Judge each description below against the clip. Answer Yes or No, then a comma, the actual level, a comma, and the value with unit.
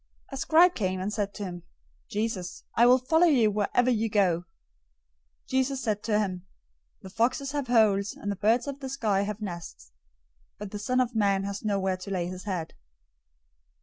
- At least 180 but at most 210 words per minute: Yes, average, 190 wpm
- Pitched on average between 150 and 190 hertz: No, high, 210 Hz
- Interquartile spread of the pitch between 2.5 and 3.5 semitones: No, average, 4.3 semitones